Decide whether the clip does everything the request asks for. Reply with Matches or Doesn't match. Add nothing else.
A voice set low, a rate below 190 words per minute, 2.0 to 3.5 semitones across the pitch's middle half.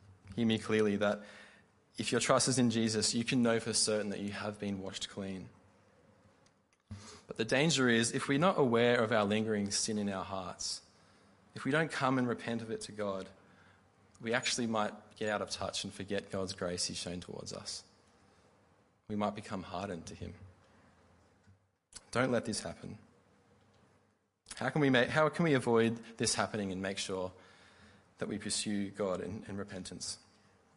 Matches